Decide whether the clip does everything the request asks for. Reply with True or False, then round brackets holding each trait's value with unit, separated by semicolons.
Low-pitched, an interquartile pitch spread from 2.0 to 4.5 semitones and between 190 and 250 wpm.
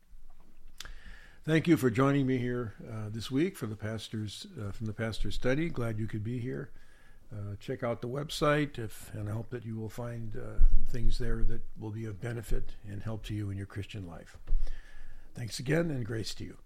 True (115 Hz; 2.8 semitones; 205 wpm)